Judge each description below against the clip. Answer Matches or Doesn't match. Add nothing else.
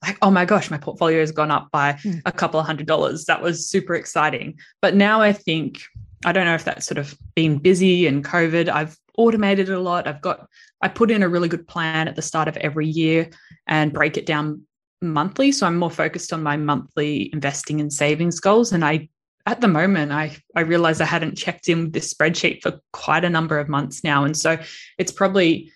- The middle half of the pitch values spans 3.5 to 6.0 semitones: Doesn't match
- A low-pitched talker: Doesn't match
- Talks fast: Matches